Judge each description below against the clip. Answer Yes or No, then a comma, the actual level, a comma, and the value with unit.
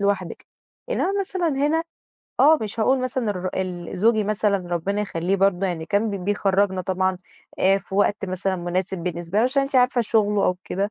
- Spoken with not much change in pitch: No, average, 3.4 semitones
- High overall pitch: Yes, high, 200 Hz